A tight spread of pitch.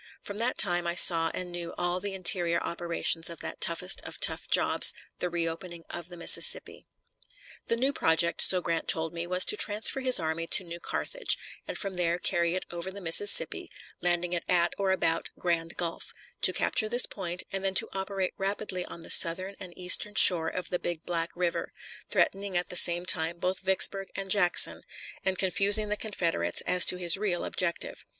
Yes: narrow, 2.2 semitones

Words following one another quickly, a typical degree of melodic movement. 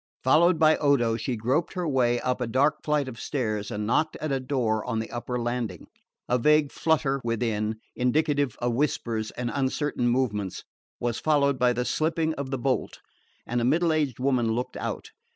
No: average, 185 wpm; average, 3.6 semitones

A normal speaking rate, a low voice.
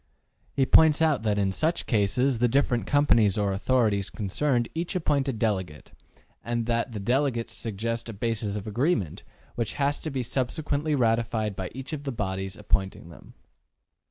Yes: average, 170 wpm; low, 115 Hz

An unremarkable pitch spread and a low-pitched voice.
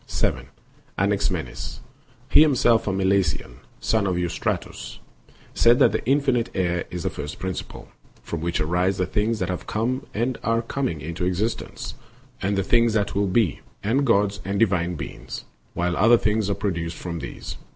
Yes: average, 4.5 semitones; low, 100 Hz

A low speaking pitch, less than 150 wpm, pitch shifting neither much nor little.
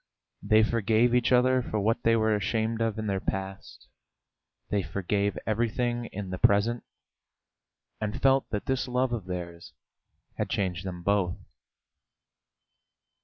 Yes: low, 110 Hz; slow, 135 wpm; average, 3.4 semitones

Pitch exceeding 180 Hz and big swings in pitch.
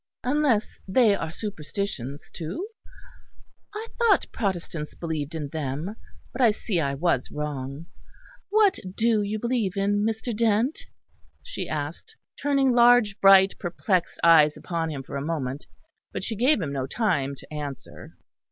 Yes: high, 190 Hz; wide, 7.3 semitones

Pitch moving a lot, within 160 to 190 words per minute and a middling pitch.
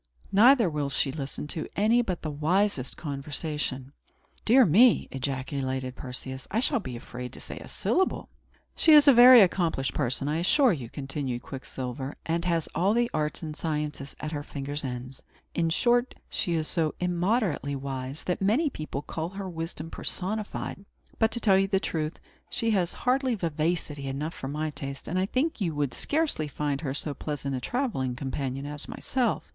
Yes: wide, 6.3 semitones; average, 175 wpm; medium, 155 Hz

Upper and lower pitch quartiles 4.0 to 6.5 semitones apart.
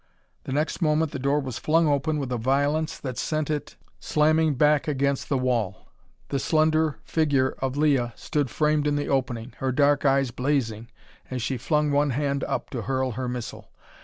No: average, 2.8 semitones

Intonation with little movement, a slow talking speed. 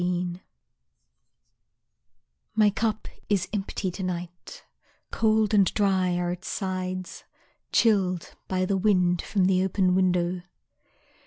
Yes: narrow, 1.9 semitones; slow, 110 wpm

